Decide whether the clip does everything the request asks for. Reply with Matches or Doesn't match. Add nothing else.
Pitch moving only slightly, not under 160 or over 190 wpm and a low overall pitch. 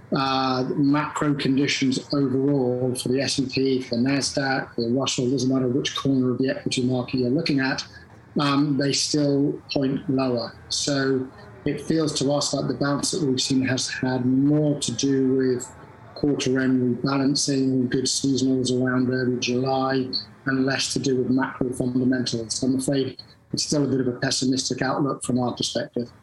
Matches